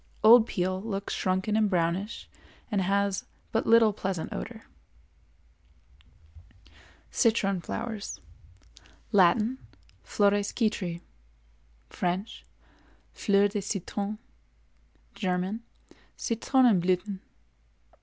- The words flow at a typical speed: No, slow, 65 wpm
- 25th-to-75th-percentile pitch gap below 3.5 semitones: Yes, average, 2.7 semitones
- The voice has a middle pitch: No, high, 200 Hz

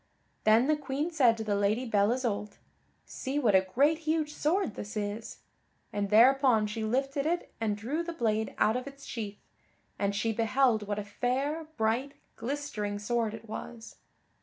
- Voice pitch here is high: Yes, high, 230 Hz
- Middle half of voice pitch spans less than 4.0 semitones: No, average, 4.6 semitones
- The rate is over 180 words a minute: No, average, 170 wpm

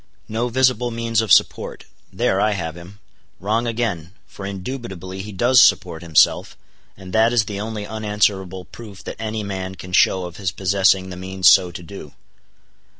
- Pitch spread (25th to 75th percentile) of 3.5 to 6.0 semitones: No, average, 3.1 semitones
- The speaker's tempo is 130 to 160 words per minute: No, average, 170 wpm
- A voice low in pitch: Yes, low, 100 Hz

